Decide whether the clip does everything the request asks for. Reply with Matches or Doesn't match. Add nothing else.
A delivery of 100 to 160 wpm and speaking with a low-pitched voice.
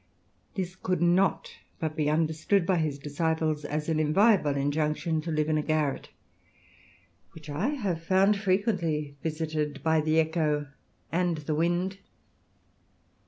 Doesn't match